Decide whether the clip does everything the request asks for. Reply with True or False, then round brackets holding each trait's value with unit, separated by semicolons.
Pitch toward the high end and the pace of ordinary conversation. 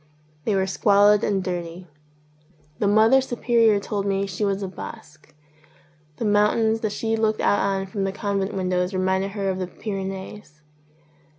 True (200 Hz; 165 wpm)